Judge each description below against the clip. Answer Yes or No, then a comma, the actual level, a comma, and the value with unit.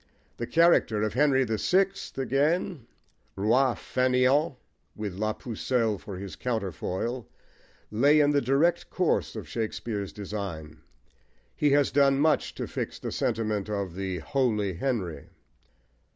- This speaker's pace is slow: Yes, slow, 130 wpm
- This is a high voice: No, low, 115 Hz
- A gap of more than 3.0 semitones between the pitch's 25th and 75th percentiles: Yes, average, 5.3 semitones